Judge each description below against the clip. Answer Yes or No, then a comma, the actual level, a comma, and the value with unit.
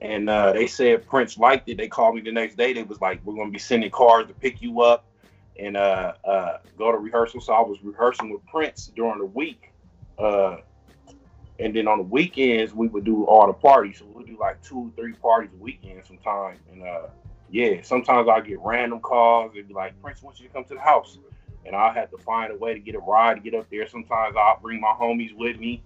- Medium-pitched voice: No, low, 115 Hz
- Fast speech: Yes, fast, 245 wpm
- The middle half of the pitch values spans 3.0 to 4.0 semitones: No, narrow, 2.6 semitones